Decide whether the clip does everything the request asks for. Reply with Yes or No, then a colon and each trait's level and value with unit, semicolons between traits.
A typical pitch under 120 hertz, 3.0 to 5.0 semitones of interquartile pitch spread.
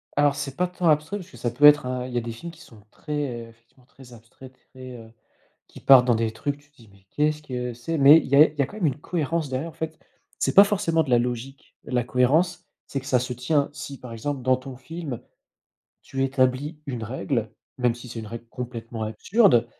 No: low, 130 Hz; average, 3.7 semitones